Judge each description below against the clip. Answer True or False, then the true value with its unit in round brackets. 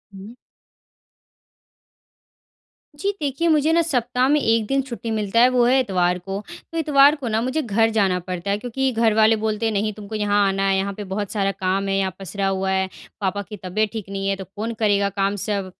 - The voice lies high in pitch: True (210 Hz)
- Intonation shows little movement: False (3.9 semitones)